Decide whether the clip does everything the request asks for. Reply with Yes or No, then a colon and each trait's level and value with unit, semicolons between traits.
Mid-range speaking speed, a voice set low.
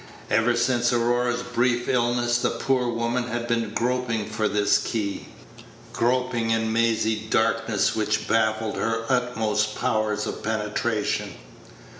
No: slow, 125 wpm; low, 115 Hz